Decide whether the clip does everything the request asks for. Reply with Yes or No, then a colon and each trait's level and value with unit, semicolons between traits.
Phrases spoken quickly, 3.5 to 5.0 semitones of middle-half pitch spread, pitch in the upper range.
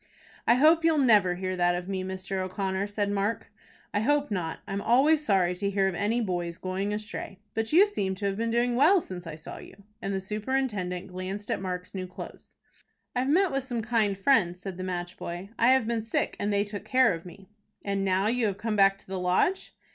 Yes: fast, 225 wpm; average, 3.9 semitones; high, 200 Hz